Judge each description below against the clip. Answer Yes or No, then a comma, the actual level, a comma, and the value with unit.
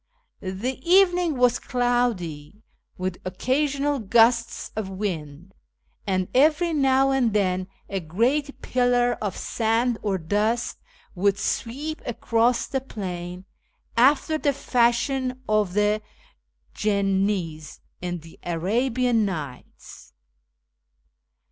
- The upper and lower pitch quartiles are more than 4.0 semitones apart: Yes, average, 5.3 semitones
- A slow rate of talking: Yes, slow, 100 wpm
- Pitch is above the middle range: Yes, high, 225 Hz